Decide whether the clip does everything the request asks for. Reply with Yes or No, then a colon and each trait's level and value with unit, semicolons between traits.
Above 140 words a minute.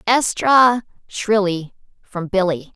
No: slow, 85 wpm